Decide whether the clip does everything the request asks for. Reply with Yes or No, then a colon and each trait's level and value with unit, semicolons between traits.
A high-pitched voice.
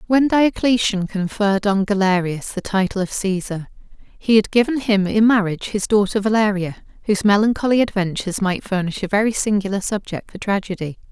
Yes: high, 205 Hz